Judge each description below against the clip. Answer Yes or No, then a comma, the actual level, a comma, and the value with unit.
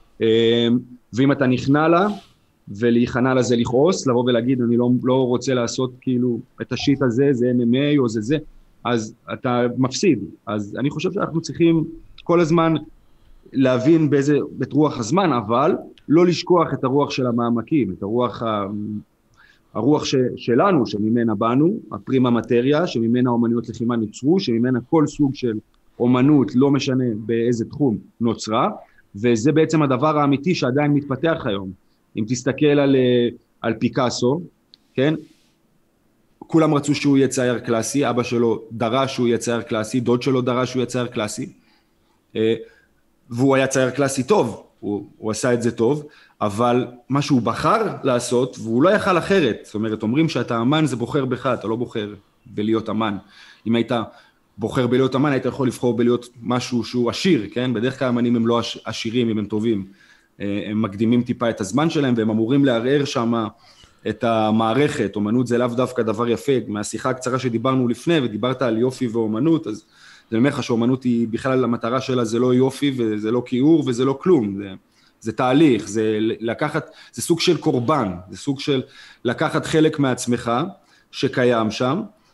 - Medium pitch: No, low, 125 Hz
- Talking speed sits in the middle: No, fast, 160 wpm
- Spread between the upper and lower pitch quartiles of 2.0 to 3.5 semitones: Yes, average, 3.1 semitones